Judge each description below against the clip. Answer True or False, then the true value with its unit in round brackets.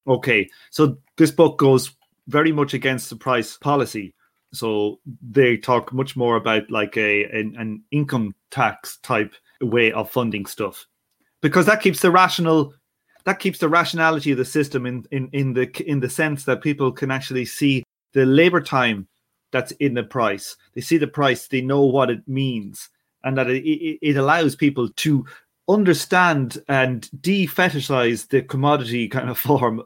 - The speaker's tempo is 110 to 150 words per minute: False (165 wpm)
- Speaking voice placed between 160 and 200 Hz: False (135 Hz)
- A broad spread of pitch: False (3.5 semitones)